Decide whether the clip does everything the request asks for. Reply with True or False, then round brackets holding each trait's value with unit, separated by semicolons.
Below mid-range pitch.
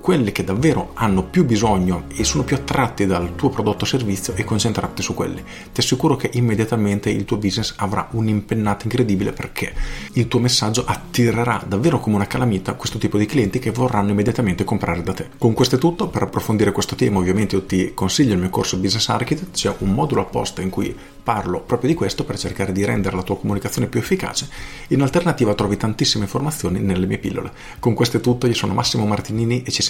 True (105 Hz)